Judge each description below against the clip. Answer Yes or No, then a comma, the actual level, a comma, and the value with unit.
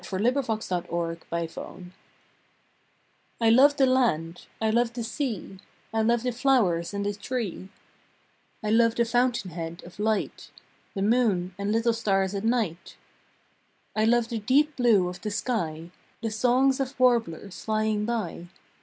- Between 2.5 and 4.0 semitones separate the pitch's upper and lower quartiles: No, average, 4.4 semitones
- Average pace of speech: Yes, average, 155 wpm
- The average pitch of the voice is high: Yes, high, 220 Hz